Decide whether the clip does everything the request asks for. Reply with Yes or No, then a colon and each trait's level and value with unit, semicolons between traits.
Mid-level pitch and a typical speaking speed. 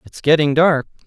Yes: medium, 155 Hz; average, 170 wpm